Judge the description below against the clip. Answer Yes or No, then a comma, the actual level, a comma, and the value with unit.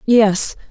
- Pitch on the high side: Yes, high, 215 Hz